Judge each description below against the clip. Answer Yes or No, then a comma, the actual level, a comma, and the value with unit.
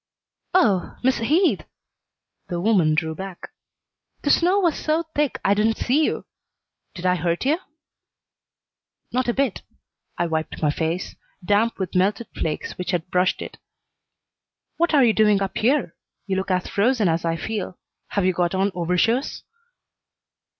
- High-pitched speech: Yes, high, 195 Hz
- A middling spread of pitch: No, wide, 5.8 semitones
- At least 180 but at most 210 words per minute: No, average, 155 wpm